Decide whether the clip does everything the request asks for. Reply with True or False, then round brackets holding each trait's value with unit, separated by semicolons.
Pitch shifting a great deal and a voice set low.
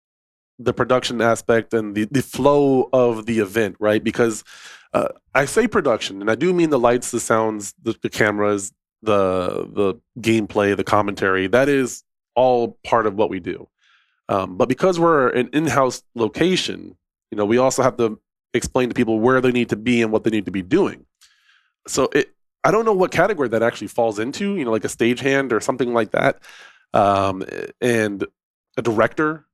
False (3.3 semitones; 115 Hz)